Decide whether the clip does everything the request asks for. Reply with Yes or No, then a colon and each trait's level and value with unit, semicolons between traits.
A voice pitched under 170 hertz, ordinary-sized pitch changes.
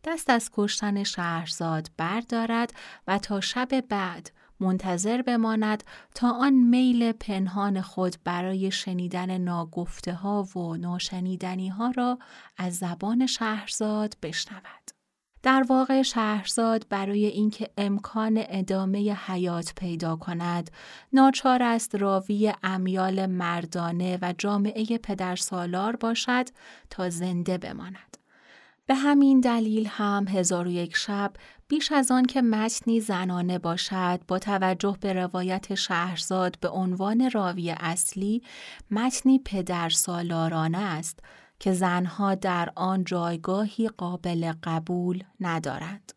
No: high, 195 Hz; average, 3.9 semitones